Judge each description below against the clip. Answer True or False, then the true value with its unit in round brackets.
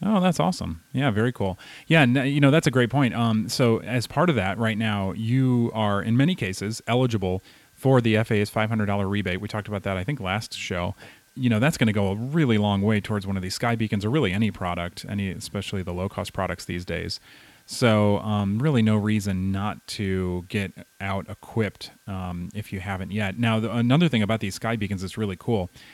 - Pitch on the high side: False (105 Hz)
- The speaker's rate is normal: False (220 wpm)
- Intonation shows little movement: False (3.2 semitones)